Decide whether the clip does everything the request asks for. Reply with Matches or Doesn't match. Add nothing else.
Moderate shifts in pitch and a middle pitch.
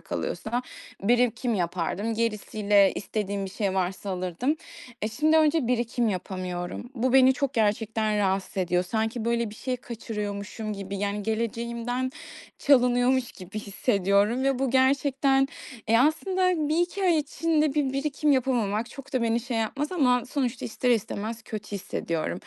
Doesn't match